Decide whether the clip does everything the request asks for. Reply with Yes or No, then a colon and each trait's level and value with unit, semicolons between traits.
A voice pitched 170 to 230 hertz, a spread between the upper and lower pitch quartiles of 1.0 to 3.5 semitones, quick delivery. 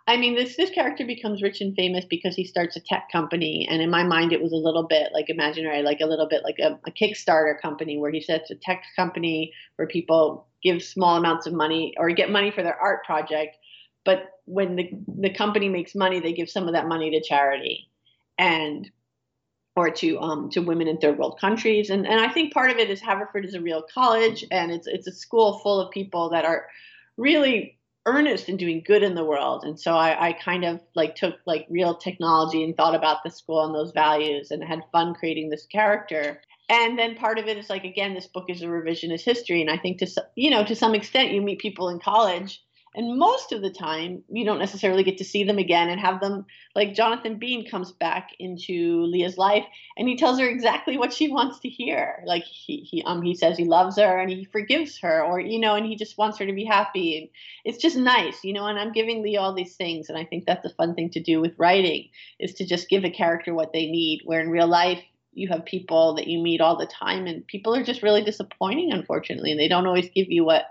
No: medium, 185 Hz; average, 4.3 semitones; fast, 240 wpm